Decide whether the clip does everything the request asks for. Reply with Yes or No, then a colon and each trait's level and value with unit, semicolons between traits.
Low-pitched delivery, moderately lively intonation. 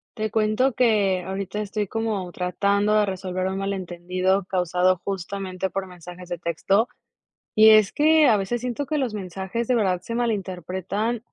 No: high, 195 Hz; average, 3.0 semitones